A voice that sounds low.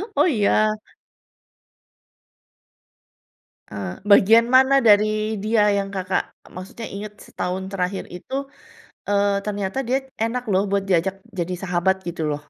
No: high, 200 Hz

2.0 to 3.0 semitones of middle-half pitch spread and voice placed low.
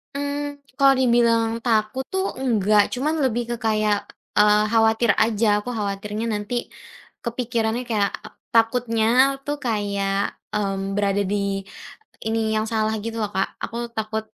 No: narrow, 2.5 semitones; high, 220 Hz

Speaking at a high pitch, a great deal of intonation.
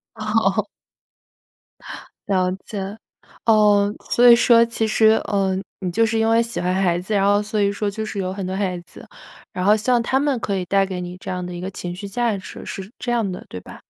No: high, 200 Hz; average, 3.0 semitones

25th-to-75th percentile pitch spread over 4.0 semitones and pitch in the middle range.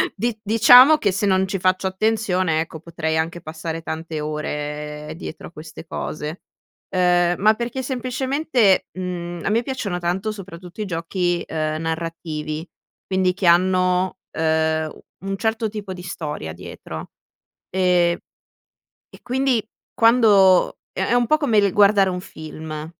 Yes: average, 4.6 semitones; medium, 180 Hz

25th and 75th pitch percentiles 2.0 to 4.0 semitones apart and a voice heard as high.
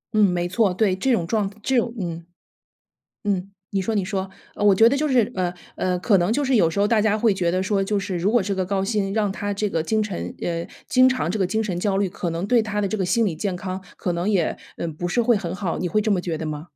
Yes: average, 3.2 semitones; high, 195 Hz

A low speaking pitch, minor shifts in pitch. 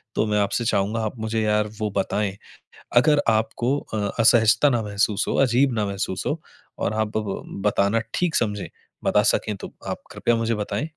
Yes: low, 110 Hz; narrow, 2.2 semitones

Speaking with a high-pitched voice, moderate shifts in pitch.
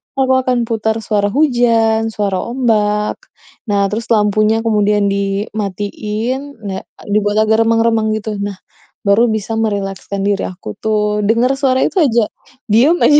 No: high, 215 Hz; narrow, 2.2 semitones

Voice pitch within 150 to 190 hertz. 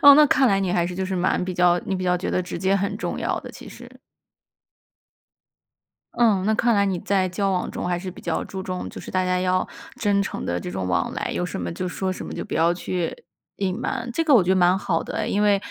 Yes: medium, 185 Hz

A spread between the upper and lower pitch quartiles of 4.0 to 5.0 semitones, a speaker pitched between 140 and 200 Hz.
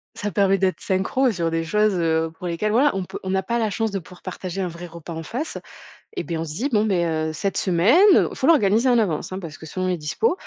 Yes: average, 4.5 semitones; high, 190 Hz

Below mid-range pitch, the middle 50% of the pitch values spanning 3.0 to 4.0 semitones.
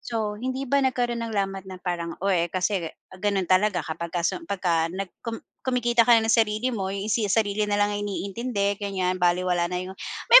No: high, 200 Hz; average, 3.7 semitones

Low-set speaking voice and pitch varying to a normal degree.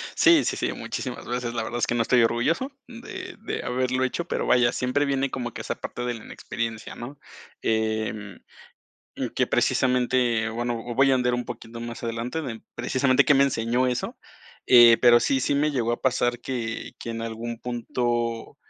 No: low, 120 Hz; narrow, 1.9 semitones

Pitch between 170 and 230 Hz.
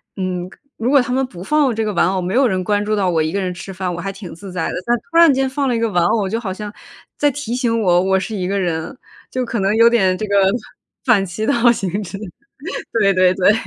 Yes: high, 205 Hz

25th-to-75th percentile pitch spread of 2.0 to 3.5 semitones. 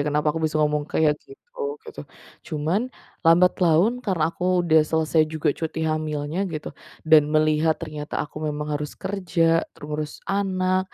Yes: average, 3.1 semitones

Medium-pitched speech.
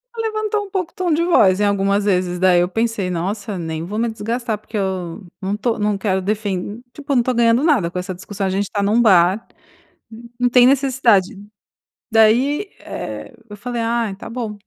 No: high, 215 Hz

